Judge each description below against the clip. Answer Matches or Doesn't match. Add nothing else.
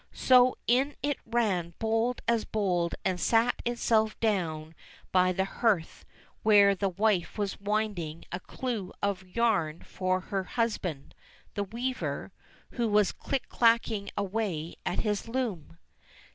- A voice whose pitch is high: Matches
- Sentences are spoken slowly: Matches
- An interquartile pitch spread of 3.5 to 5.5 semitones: Matches